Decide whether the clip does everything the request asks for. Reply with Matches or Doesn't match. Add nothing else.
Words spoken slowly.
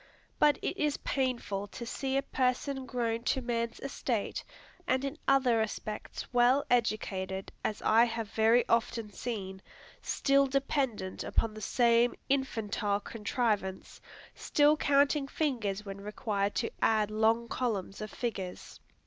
Matches